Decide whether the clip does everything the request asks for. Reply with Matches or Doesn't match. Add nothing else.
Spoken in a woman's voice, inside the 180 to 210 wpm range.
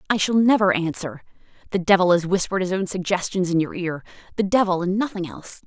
Matches